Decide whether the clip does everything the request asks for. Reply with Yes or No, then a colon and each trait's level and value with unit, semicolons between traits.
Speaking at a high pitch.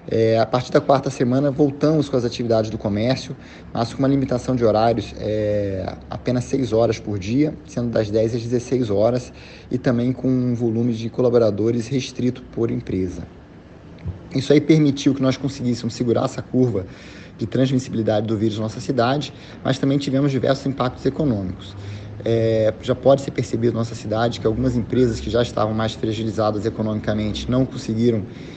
No: low, 120 Hz